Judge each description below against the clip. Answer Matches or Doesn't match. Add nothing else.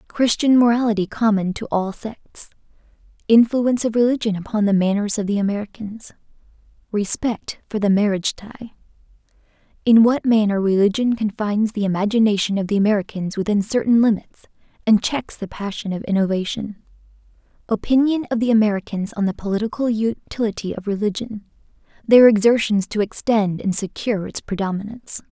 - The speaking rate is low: Matches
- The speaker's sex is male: Doesn't match